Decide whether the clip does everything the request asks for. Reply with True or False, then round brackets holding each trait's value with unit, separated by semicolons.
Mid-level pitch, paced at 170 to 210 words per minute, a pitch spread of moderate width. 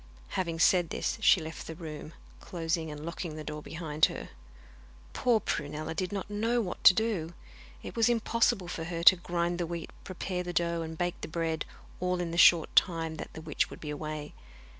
False (170 Hz; 200 wpm; 2.3 semitones)